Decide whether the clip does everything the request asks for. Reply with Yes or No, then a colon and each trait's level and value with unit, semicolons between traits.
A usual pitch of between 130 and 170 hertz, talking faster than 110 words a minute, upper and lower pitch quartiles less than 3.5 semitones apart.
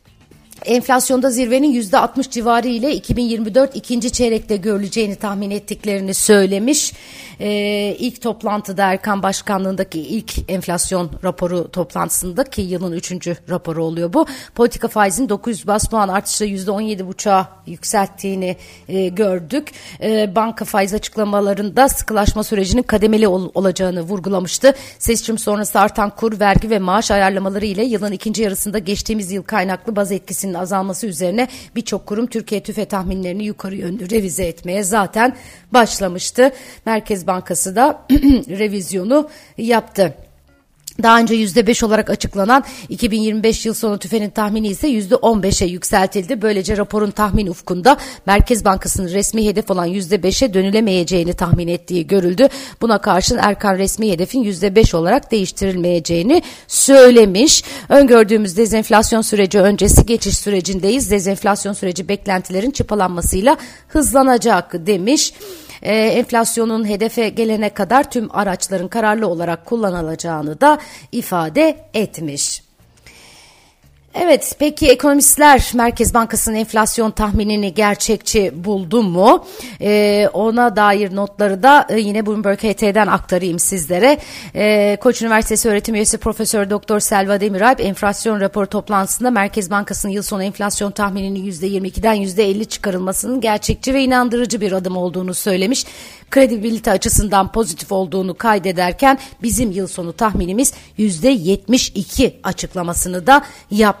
No: high, 210 Hz; average, 120 wpm; average, 3.1 semitones